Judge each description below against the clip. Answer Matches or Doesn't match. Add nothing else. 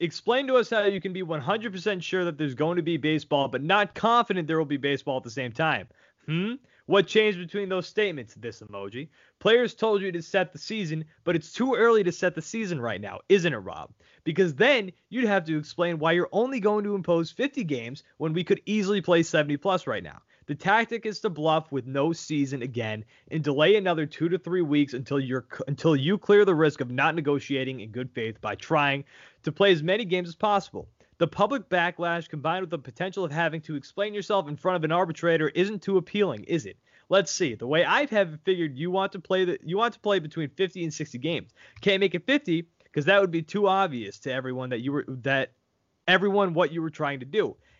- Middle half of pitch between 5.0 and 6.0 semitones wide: Matches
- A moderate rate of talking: Doesn't match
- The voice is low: Doesn't match